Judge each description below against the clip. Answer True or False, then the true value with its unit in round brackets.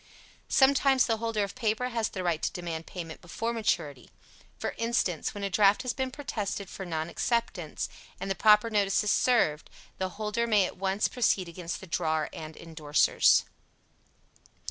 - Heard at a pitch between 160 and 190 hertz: False (200 Hz)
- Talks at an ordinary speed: True (165 wpm)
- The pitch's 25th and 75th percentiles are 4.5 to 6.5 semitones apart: True (5.0 semitones)